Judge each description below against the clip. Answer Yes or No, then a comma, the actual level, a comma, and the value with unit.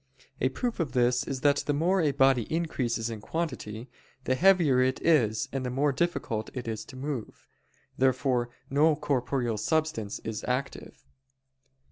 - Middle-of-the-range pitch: No, low, 130 Hz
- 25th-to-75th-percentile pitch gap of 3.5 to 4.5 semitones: Yes, average, 3.8 semitones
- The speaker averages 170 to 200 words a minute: No, average, 145 wpm